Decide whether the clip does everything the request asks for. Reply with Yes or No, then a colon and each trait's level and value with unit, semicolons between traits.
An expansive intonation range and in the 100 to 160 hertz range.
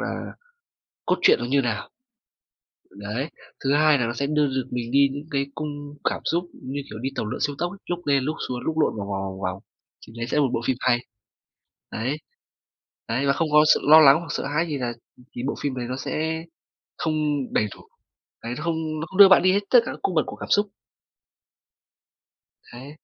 No: average, 4.2 semitones; medium, 140 Hz